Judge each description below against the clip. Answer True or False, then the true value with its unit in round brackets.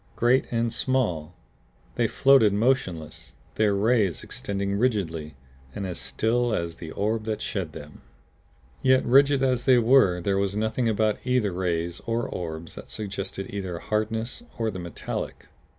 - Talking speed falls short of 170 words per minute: True (150 wpm)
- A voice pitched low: True (105 Hz)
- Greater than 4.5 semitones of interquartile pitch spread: True (5.0 semitones)